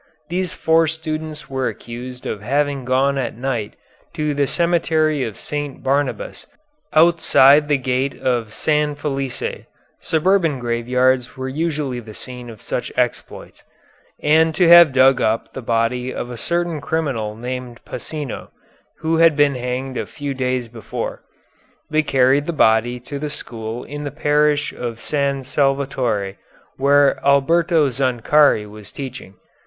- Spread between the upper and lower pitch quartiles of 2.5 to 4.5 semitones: Yes, average, 3.4 semitones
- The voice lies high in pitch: No, low, 135 Hz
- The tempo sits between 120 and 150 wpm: Yes, average, 140 wpm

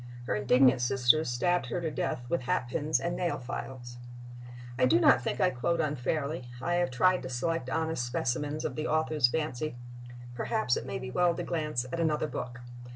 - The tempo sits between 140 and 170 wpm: No, average, 185 wpm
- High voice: No, medium, 140 Hz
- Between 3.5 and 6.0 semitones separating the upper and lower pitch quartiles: Yes, average, 4.6 semitones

